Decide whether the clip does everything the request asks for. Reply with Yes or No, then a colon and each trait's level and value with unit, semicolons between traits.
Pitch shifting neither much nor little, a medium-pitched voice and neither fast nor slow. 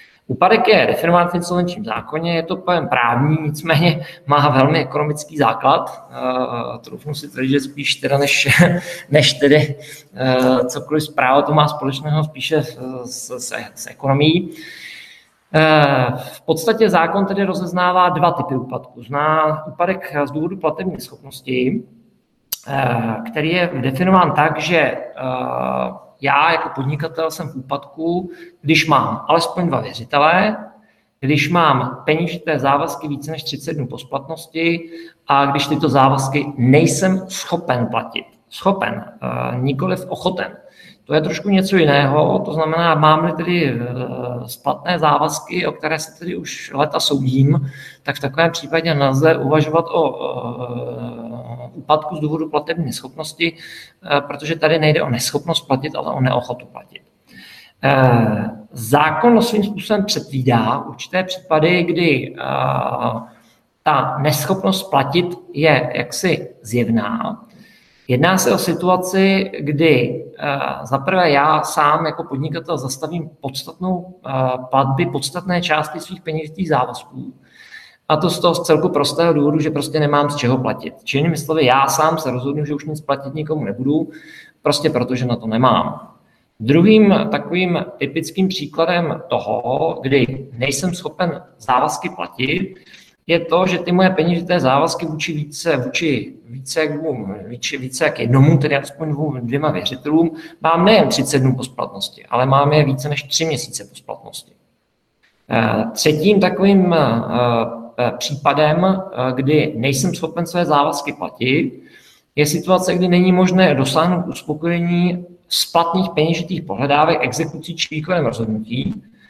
Yes: average, 3.9 semitones; medium, 155 Hz; average, 130 wpm